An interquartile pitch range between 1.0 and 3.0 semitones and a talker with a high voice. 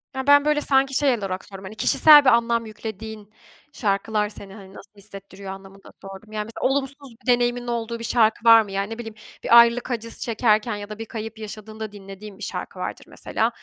Yes: average, 2.7 semitones; high, 220 Hz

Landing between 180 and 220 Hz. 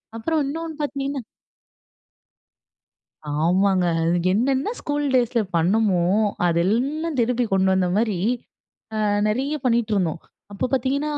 No: high, 235 Hz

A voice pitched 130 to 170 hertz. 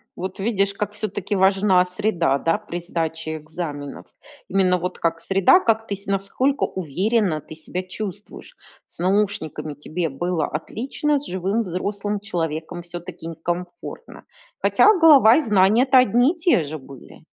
No: medium, 185 Hz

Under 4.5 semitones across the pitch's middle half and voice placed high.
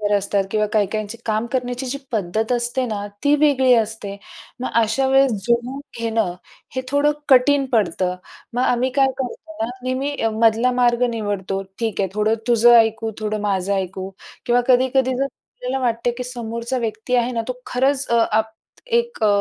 Yes: average, 3.0 semitones; high, 235 Hz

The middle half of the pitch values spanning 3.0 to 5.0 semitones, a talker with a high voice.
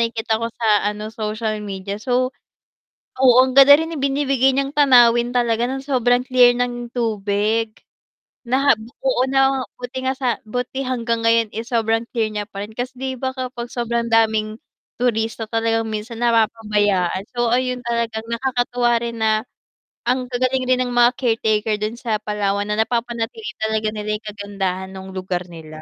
No: narrow, 2.6 semitones; high, 235 Hz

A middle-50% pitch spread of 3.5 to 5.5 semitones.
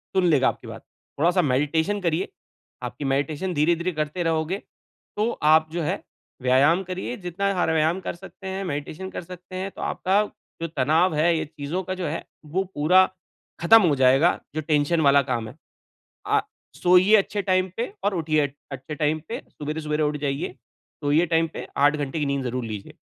Yes: average, 4.0 semitones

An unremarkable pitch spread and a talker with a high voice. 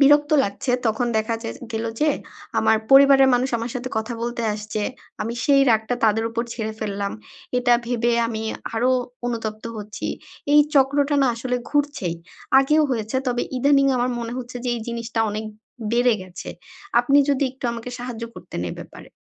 Yes: average, 3.3 semitones; high, 240 Hz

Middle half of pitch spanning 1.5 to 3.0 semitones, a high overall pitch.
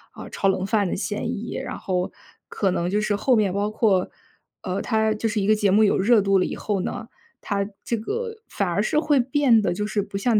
Yes: narrow, 2.5 semitones; high, 210 Hz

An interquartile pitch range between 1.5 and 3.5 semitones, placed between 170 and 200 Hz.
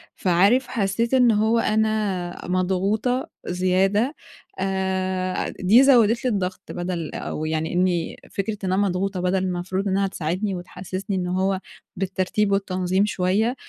Yes: narrow, 2.4 semitones; high, 190 Hz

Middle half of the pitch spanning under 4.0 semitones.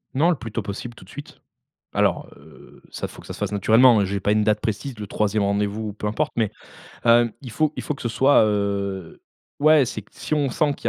No: average, 4.3 semitones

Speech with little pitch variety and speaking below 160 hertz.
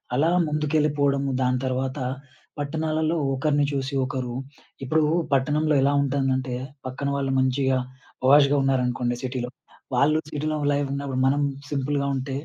Yes: narrow, 2.0 semitones; medium, 140 Hz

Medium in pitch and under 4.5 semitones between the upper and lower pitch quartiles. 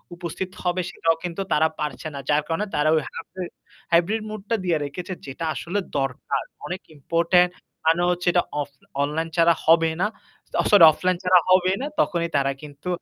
Yes: medium, 170 Hz; average, 2.9 semitones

